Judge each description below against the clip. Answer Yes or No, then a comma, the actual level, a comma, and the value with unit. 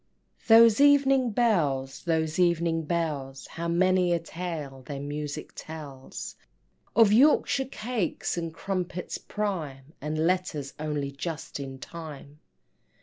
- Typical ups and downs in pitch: Yes, average, 4.4 semitones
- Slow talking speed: Yes, slow, 115 wpm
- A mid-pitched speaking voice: Yes, medium, 165 Hz